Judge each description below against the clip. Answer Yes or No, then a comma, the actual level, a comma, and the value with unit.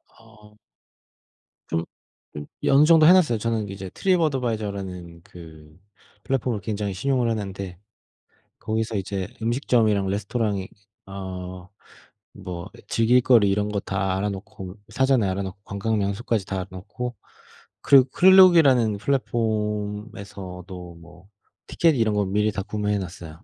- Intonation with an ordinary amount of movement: Yes, average, 3.5 semitones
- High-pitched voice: No, low, 105 Hz